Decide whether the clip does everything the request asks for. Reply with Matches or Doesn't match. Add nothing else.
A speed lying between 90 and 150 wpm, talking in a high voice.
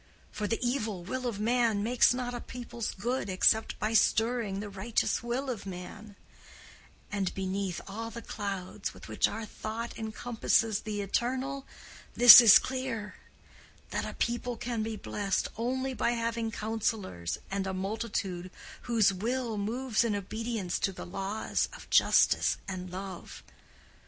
Matches